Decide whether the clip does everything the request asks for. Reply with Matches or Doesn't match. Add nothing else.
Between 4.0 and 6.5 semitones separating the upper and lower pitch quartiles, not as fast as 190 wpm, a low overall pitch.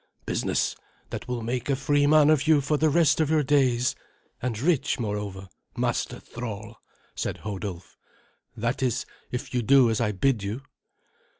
Matches